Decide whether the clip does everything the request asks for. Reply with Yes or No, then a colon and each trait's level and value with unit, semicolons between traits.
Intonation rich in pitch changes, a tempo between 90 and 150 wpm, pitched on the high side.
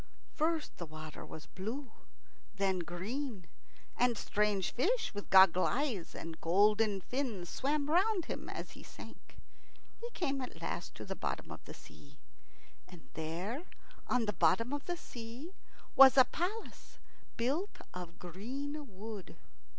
Yes: wide, 7.3 semitones; average, 145 wpm; high, 230 Hz